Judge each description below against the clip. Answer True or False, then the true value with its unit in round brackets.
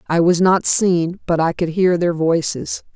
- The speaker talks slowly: False (205 wpm)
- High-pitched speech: False (170 Hz)